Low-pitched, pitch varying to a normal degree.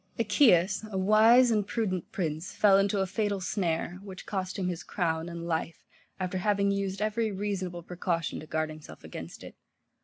No: high, 190 Hz; average, 3.1 semitones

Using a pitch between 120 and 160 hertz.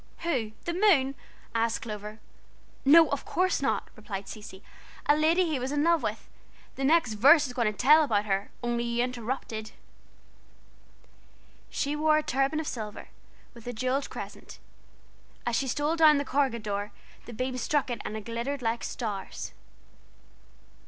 No: very high, 255 Hz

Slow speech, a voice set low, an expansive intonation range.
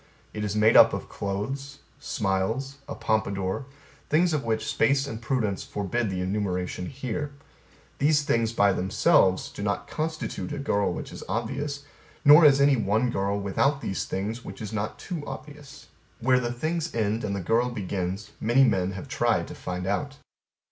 No: average, 170 wpm; low, 115 Hz; wide, 5.7 semitones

